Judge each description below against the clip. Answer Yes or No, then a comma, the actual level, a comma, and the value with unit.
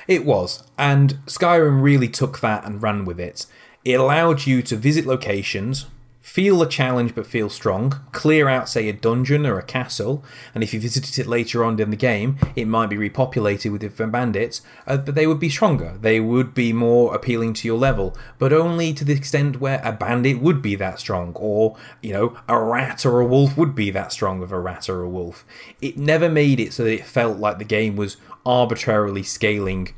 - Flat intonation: No, average, 4.2 semitones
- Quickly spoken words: Yes, fast, 210 wpm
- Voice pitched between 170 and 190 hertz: No, low, 120 Hz